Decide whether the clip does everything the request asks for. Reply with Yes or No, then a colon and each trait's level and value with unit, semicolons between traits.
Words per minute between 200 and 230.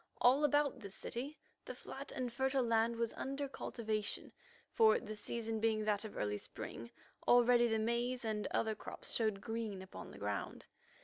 No: average, 170 wpm